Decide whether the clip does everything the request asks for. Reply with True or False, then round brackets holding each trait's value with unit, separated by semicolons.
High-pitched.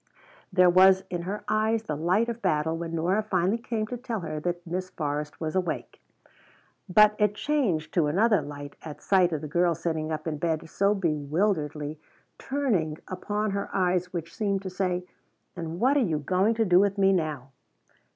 False (180 Hz)